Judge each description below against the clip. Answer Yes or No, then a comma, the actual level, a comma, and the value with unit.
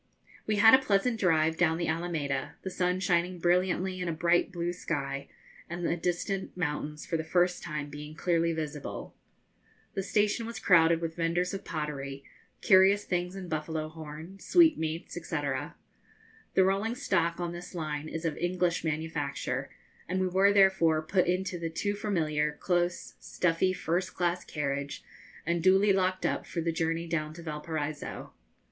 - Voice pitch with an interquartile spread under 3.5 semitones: Yes, average, 2.8 semitones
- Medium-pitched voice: Yes, medium, 170 Hz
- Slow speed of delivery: No, average, 160 wpm